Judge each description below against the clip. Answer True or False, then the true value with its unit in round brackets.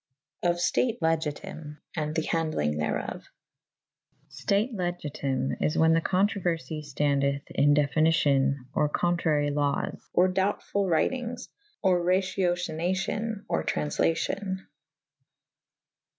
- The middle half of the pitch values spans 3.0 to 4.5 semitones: True (4.2 semitones)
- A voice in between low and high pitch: True (165 Hz)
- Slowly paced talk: True (110 wpm)